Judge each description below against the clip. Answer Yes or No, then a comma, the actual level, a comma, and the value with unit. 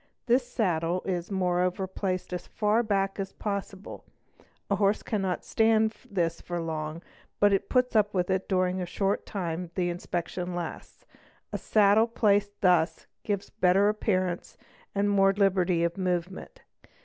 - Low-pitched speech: No, high, 190 Hz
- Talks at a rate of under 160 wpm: Yes, average, 150 wpm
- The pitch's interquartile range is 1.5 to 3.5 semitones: Yes, narrow, 2.5 semitones